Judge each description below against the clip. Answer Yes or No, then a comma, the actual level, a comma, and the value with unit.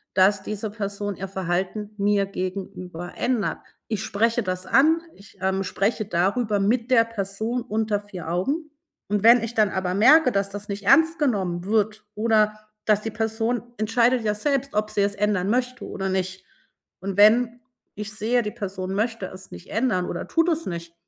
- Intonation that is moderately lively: Yes, average, 3.1 semitones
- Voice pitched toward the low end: No, high, 210 Hz